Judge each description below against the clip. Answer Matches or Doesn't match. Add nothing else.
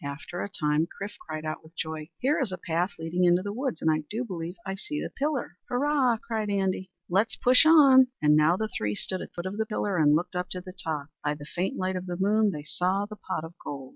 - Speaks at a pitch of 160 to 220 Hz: Matches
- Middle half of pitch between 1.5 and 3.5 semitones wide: Doesn't match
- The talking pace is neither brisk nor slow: Doesn't match